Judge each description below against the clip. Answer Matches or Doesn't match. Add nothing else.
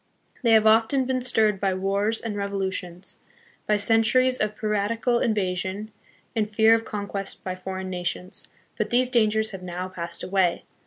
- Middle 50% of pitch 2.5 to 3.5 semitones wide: Matches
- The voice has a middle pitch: Doesn't match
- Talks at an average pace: Matches